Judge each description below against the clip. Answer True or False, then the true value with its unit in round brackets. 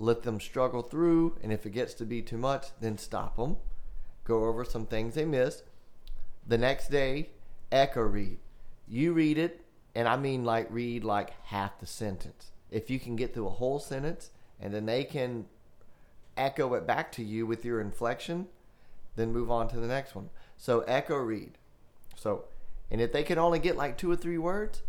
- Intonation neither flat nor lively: True (4.0 semitones)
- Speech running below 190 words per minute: False (195 wpm)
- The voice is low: True (120 Hz)